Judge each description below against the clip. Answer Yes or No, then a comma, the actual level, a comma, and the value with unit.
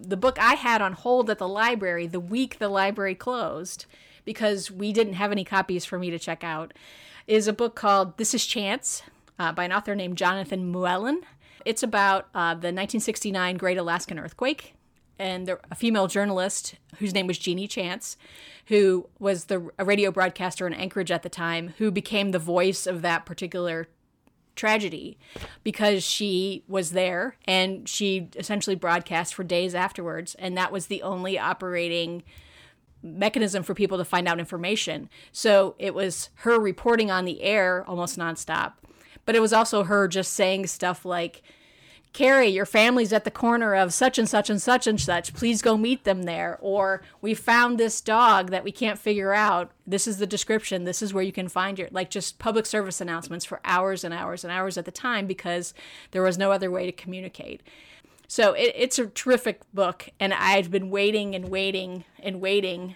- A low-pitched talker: No, high, 195 Hz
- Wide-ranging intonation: No, average, 2.7 semitones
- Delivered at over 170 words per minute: Yes, average, 185 wpm